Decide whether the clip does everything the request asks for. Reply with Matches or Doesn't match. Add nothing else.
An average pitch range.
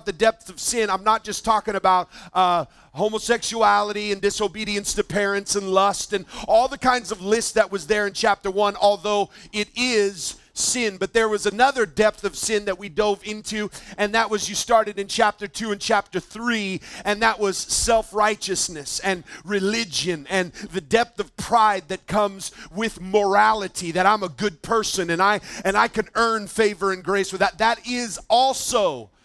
Doesn't match